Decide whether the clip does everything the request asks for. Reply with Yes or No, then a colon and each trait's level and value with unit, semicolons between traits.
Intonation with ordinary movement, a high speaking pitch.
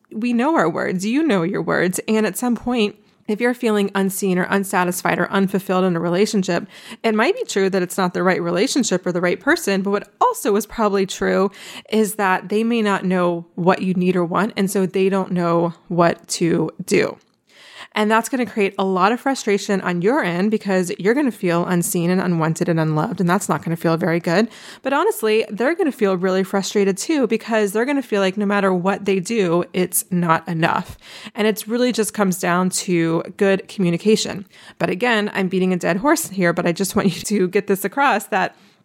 Yes: average, 3.0 semitones; high, 195 Hz